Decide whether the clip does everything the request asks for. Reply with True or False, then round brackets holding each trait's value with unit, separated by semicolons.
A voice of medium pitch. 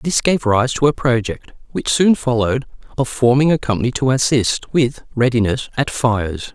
False (125 Hz)